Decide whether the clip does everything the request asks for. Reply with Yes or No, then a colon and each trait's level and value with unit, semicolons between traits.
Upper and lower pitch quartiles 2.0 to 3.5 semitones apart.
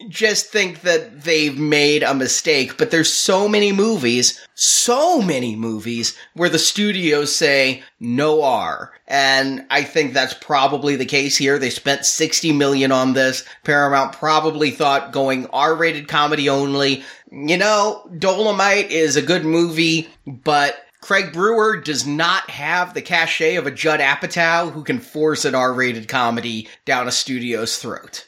No: average, 4.2 semitones